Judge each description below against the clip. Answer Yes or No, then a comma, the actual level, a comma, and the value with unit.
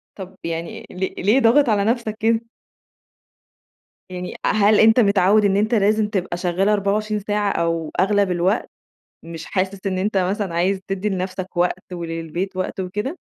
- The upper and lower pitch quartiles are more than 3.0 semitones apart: No, narrow, 2.6 semitones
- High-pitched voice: Yes, high, 195 Hz